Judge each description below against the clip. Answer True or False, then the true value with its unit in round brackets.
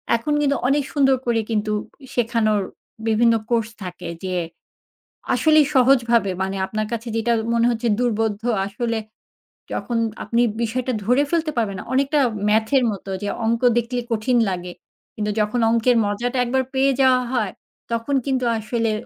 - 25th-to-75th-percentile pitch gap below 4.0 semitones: True (2.9 semitones)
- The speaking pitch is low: False (235 Hz)